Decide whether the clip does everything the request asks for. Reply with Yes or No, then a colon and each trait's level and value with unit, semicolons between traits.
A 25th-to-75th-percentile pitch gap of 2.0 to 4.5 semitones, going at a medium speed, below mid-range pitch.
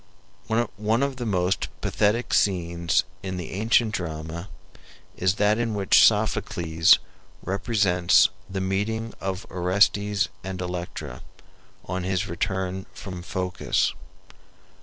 No: average, 2.7 semitones; slow, 110 wpm; very low, 95 Hz